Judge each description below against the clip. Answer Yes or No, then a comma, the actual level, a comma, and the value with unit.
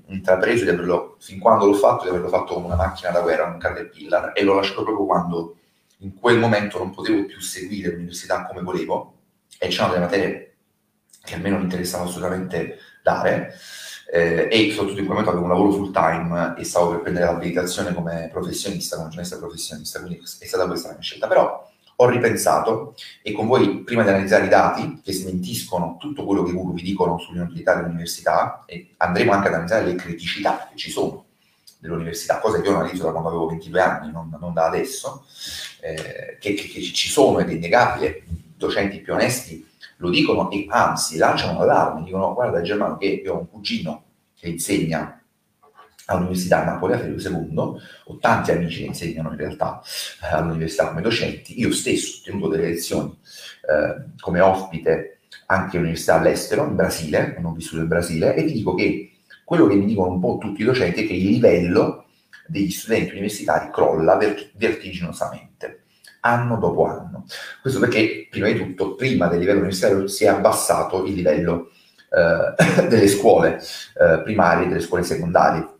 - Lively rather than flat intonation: No, narrow, 2.6 semitones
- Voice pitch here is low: Yes, very low, 90 Hz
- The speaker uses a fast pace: Yes, fast, 180 wpm